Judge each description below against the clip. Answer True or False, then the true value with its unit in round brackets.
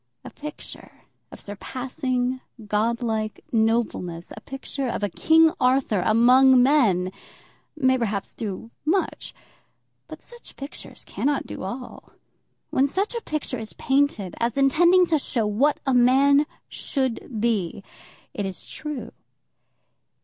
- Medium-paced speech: False (125 wpm)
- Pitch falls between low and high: False (255 Hz)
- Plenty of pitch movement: False (4.4 semitones)